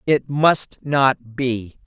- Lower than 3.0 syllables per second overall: Yes, 2.5 syllables/s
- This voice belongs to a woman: Yes, female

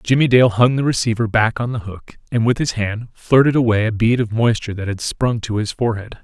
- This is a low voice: Yes, low, 115 Hz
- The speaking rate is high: Yes, fast, 230 wpm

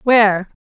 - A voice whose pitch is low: No, high, 210 Hz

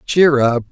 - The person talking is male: Yes, male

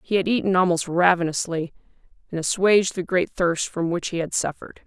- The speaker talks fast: No, average, 185 wpm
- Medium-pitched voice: Yes, medium, 175 Hz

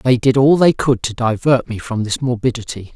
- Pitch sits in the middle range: No, low, 120 Hz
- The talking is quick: Yes, fast, 225 wpm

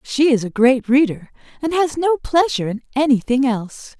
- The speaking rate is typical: Yes, average, 180 wpm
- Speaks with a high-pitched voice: Yes, very high, 265 Hz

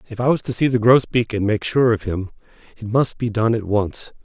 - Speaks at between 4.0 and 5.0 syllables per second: No, 5.4 syllables/s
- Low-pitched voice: Yes, low, 115 Hz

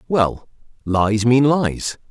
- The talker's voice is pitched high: No, low, 120 Hz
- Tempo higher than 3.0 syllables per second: No, 2.7 syllables/s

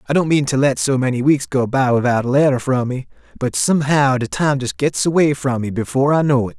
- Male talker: Yes, male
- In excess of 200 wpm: Yes, fast, 255 wpm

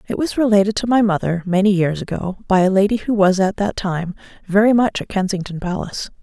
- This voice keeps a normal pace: No, fast, 210 wpm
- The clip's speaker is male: No, female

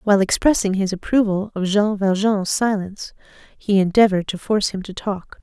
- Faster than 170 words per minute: No, average, 165 wpm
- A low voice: No, high, 200 Hz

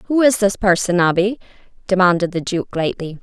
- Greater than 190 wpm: No, average, 165 wpm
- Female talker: Yes, female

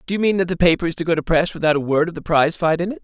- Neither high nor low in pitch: Yes, medium, 170 Hz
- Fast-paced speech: Yes, fast, 395 wpm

